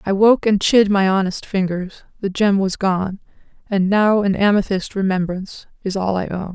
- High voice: Yes, high, 195 Hz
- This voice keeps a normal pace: Yes, average, 185 wpm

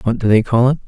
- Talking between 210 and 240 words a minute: No, fast, 340 wpm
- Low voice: Yes, low, 120 Hz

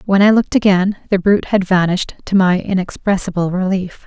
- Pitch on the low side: No, high, 190 Hz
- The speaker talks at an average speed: Yes, average, 175 wpm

